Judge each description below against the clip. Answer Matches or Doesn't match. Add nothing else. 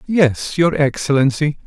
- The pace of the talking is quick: Doesn't match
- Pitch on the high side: Doesn't match